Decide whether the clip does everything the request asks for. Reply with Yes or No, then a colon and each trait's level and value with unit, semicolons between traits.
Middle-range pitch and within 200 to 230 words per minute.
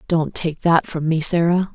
Yes: medium, 165 Hz; fast, 205 wpm